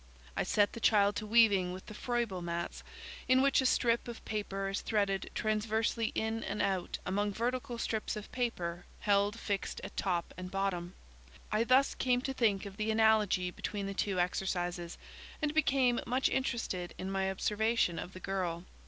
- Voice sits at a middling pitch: No, high, 205 Hz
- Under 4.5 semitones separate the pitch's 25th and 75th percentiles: Yes, average, 3.5 semitones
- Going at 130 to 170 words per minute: No, average, 180 wpm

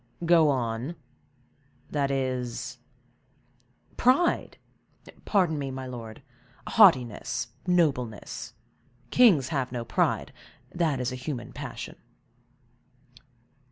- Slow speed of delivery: Yes, slow, 85 wpm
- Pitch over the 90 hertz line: Yes, low, 135 Hz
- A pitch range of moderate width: Yes, average, 4.3 semitones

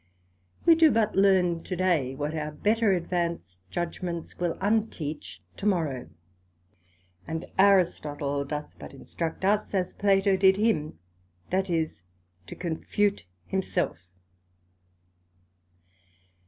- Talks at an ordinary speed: No, slow, 110 wpm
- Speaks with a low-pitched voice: No, medium, 175 Hz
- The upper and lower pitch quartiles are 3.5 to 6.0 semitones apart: Yes, average, 4.3 semitones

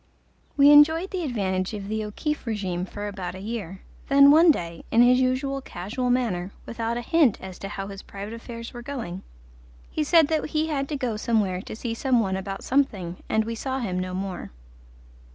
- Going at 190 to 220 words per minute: Yes, average, 200 wpm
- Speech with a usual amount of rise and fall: No, wide, 5.9 semitones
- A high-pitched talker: Yes, high, 230 Hz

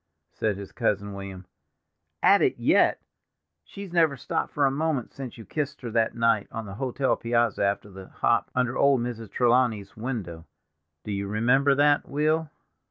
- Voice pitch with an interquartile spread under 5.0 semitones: No, wide, 5.4 semitones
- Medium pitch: No, low, 120 Hz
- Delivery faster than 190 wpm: No, average, 165 wpm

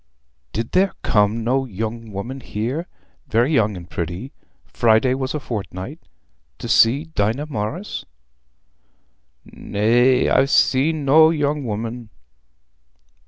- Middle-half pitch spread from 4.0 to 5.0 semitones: Yes, average, 4.7 semitones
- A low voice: Yes, low, 120 Hz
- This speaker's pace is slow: Yes, slow, 105 wpm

